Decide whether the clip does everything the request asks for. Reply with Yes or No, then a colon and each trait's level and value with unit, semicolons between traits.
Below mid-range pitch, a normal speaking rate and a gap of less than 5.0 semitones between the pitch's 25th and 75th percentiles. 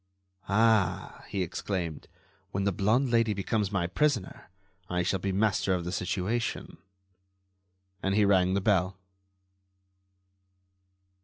No: low, 100 Hz; slow, 120 wpm; average, 2.8 semitones